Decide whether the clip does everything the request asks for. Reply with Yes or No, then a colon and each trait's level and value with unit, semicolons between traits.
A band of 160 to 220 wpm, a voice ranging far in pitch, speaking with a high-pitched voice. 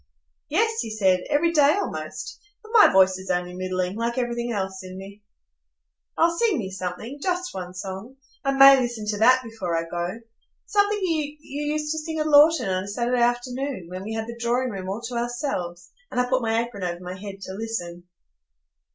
Yes: average, 190 wpm; wide, 6.6 semitones; high, 230 Hz